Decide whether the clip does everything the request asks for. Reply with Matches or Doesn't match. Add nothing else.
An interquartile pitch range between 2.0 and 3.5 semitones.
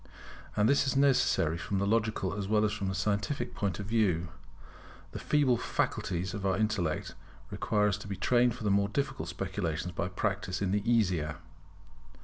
Matches